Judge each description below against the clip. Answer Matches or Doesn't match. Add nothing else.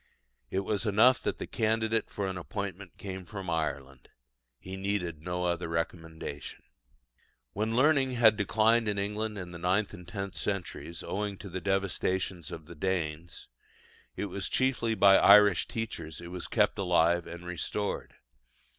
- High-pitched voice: Doesn't match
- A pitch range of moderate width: Matches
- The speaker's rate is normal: Matches